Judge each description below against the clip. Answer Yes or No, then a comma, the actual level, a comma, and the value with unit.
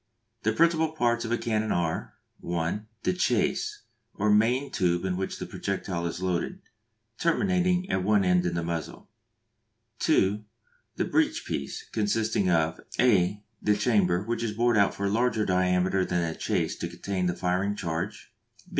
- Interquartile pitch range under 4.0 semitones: No, average, 4.6 semitones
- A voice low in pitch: Yes, low, 100 Hz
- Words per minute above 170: No, average, 165 wpm